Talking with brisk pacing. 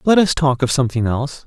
Yes: fast, 245 wpm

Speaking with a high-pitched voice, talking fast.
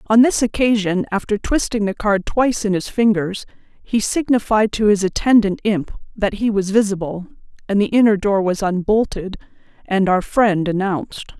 No: high, 205 Hz; average, 165 wpm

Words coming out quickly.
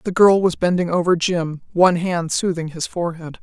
No: average, 195 wpm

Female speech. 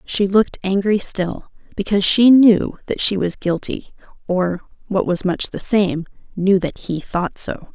Yes: female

